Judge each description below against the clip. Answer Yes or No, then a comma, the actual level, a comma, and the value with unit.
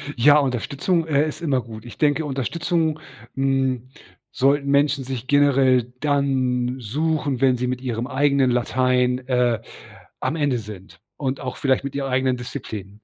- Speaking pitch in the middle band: No, low, 130 Hz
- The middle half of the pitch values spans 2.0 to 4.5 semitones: Yes, narrow, 2.4 semitones